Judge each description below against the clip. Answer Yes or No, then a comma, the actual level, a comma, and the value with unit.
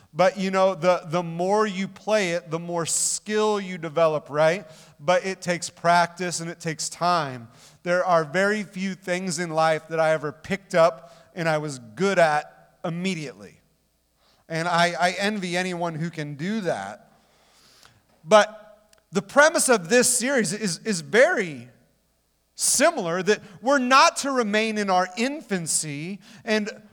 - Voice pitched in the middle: Yes, medium, 180 Hz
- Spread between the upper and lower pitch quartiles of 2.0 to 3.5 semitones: No, average, 4.2 semitones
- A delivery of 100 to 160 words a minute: Yes, average, 155 wpm